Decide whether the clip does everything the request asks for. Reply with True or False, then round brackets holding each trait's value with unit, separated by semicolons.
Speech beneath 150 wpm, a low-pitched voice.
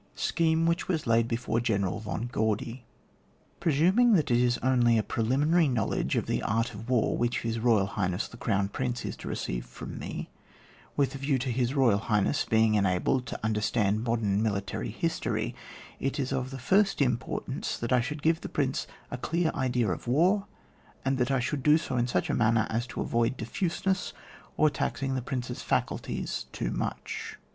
False (185 wpm; 125 Hz)